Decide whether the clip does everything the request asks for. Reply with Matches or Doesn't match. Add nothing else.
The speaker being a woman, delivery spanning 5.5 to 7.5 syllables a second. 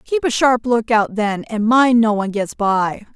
Doesn't match